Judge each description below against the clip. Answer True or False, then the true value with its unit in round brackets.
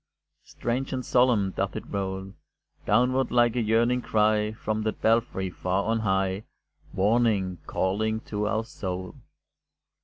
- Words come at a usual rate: False (130 wpm)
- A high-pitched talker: False (110 Hz)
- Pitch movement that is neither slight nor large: True (3.4 semitones)